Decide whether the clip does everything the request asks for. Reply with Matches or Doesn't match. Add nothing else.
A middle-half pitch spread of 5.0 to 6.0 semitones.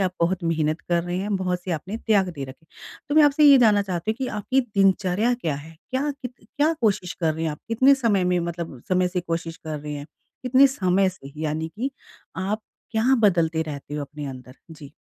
Matches